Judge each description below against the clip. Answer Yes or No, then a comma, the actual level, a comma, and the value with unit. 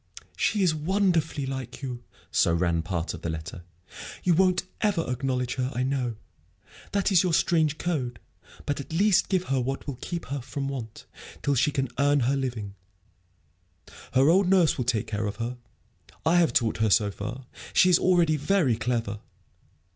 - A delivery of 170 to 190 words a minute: Yes, average, 175 wpm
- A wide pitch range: Yes, wide, 5.8 semitones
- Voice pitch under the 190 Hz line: Yes, low, 135 Hz